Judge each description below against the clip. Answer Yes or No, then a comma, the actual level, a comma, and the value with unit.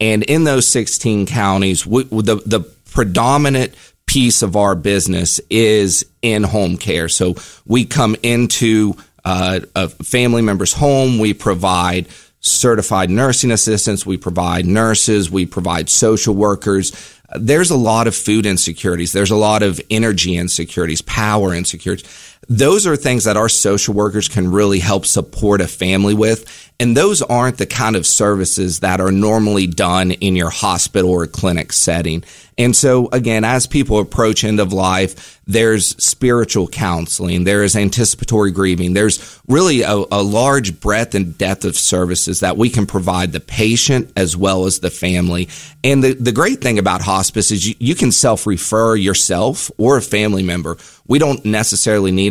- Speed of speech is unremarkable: Yes, average, 165 wpm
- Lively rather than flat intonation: No, average, 3.5 semitones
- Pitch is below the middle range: Yes, low, 105 Hz